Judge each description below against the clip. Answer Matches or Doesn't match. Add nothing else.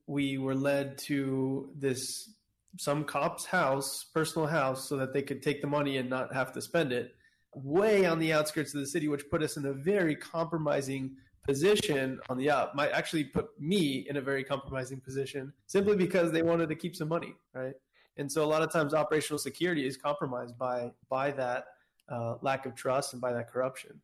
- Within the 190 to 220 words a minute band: Matches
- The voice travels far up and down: Doesn't match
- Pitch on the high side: Doesn't match